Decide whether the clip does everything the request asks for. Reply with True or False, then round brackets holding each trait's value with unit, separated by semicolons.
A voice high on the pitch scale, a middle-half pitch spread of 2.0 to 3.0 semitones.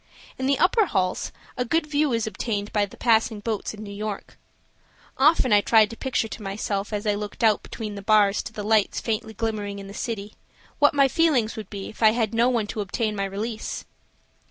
True (215 Hz; 2.4 semitones)